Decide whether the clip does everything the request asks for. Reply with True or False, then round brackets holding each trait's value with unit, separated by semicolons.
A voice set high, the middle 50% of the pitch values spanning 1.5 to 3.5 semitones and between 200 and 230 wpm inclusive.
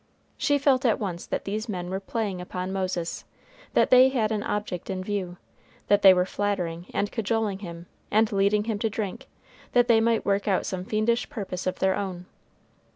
False (200 Hz; 3.1 semitones; 190 wpm)